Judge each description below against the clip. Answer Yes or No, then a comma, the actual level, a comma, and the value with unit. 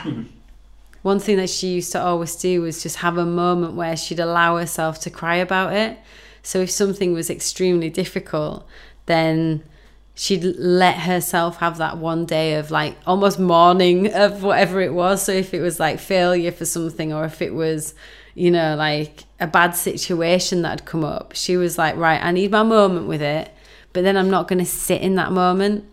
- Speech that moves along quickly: No, average, 195 wpm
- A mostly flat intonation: Yes, narrow, 2.0 semitones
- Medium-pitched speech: Yes, medium, 175 Hz